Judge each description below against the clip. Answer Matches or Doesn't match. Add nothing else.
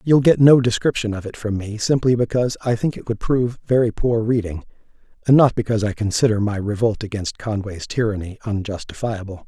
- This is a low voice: Matches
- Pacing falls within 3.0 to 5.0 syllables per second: Doesn't match